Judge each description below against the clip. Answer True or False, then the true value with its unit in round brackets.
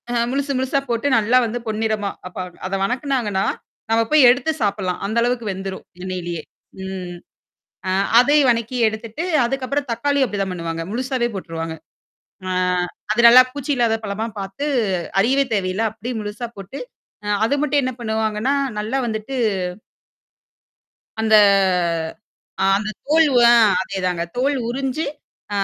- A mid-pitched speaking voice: False (225 Hz)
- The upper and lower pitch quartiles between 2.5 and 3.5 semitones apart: False (4.7 semitones)